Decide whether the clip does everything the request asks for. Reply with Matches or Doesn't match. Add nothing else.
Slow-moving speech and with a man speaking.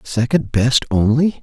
Matches